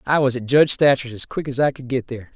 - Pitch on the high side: No, low, 130 Hz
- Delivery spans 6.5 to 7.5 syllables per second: Yes, 6.7 syllables/s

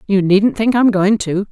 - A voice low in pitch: No, high, 205 Hz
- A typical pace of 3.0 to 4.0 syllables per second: No, 4.5 syllables/s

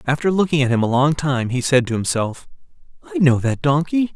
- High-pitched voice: No, medium, 140 Hz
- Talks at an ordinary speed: No, fast, 215 wpm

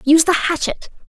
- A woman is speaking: Yes, female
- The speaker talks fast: No, average, 165 wpm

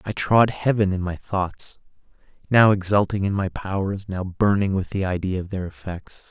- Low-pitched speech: Yes, very low, 95 Hz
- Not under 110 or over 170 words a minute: No, average, 180 wpm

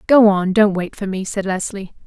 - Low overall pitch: No, high, 200 Hz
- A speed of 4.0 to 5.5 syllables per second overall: Yes, 4.9 syllables/s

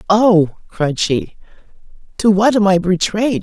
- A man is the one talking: No, female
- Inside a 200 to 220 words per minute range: No, average, 140 wpm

